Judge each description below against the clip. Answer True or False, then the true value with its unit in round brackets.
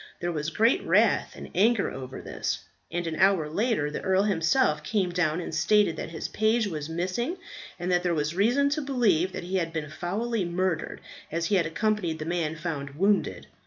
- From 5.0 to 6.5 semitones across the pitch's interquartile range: False (4.5 semitones)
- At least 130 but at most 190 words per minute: False (200 wpm)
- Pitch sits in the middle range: True (175 Hz)